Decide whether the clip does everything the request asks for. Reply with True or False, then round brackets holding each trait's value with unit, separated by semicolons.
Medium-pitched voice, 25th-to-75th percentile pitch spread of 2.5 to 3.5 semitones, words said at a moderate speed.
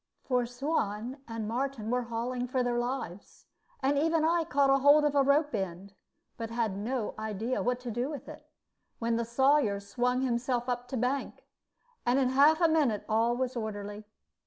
False (245 Hz; 3.2 semitones; 180 wpm)